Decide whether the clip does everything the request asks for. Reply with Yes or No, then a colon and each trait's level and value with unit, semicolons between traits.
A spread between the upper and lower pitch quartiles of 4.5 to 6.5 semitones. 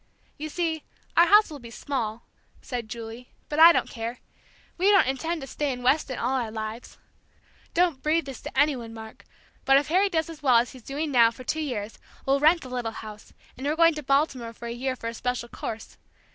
Yes: average, 4.8 semitones